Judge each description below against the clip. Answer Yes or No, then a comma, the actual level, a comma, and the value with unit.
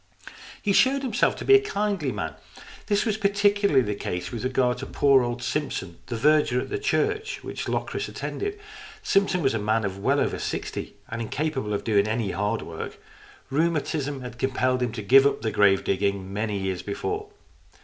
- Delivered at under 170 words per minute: No, average, 190 wpm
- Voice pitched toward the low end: Yes, low, 130 Hz